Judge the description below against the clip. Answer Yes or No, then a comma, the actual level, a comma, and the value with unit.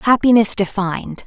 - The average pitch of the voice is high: Yes, high, 215 Hz